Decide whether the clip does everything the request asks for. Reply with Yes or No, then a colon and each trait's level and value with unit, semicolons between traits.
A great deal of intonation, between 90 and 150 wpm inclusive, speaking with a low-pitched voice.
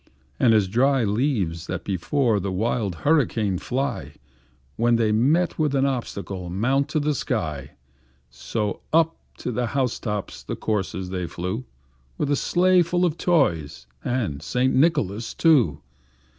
Yes: wide, 6.7 semitones; average, 145 wpm; low, 115 Hz